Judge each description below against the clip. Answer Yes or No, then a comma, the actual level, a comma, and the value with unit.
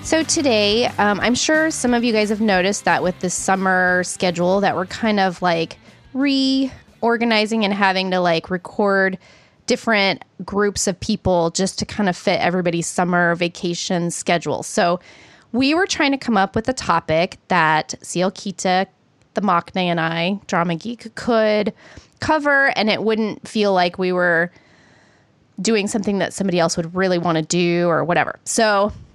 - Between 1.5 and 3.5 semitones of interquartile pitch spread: No, average, 4.0 semitones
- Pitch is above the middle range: Yes, high, 195 Hz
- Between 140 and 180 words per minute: Yes, average, 165 wpm